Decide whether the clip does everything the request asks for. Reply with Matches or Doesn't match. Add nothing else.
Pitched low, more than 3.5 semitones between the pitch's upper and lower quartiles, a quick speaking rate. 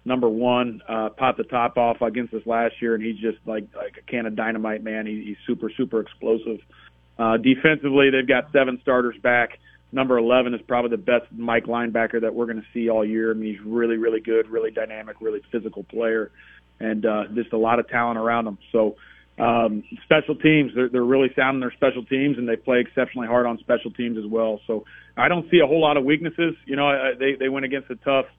Doesn't match